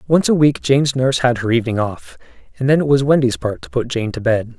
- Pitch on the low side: Yes, low, 125 Hz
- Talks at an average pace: No, fast, 260 wpm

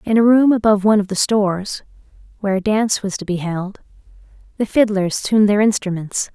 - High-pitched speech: Yes, high, 205 Hz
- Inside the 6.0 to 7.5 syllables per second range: Yes, 6.1 syllables/s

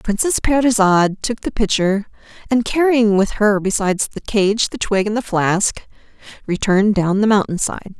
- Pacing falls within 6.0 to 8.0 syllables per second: No, 4.9 syllables/s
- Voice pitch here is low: No, high, 210 Hz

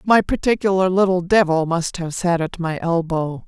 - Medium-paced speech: Yes, average, 175 wpm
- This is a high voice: No, medium, 175 Hz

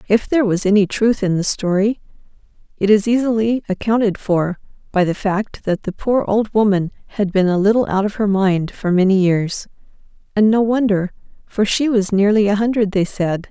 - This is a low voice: No, high, 205 Hz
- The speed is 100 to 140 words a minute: No, average, 185 wpm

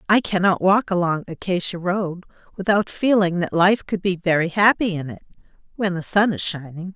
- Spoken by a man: No, female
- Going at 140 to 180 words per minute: Yes, average, 170 wpm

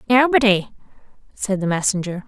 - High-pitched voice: Yes, high, 210 Hz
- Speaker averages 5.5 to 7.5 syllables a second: No, 5.3 syllables/s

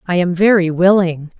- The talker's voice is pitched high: No, medium, 180 Hz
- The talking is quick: No, average, 170 wpm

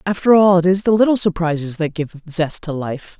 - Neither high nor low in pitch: Yes, medium, 175 Hz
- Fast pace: Yes, fast, 225 wpm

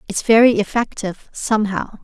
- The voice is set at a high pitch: Yes, high, 215 Hz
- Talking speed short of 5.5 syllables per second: No, 5.6 syllables/s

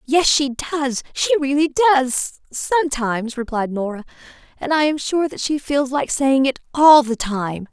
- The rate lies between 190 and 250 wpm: No, average, 165 wpm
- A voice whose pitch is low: No, very high, 275 Hz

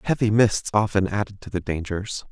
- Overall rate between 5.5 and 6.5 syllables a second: No, 5.2 syllables/s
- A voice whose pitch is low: Yes, low, 100 Hz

